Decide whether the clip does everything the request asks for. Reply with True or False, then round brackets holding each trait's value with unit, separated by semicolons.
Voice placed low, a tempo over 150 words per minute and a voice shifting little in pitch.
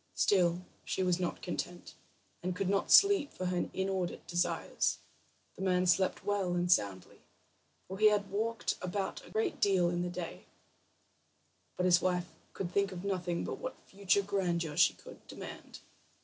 False (185 Hz; 165 wpm; 2.1 semitones)